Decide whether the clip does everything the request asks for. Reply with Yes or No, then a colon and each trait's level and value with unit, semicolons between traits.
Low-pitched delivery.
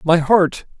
No: medium, 170 Hz